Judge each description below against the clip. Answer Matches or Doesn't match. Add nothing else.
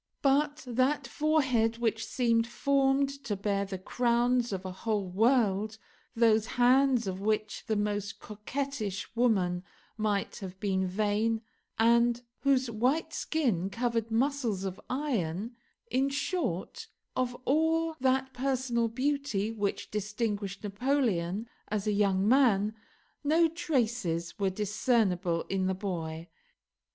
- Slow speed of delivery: Matches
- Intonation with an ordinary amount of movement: Matches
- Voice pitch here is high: Matches